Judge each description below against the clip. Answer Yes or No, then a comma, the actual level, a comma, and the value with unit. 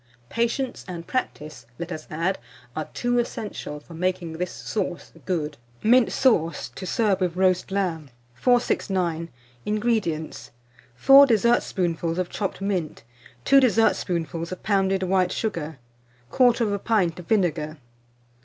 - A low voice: No, medium, 185 Hz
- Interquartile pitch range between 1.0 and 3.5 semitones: No, average, 4.8 semitones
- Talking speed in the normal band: No, slow, 125 wpm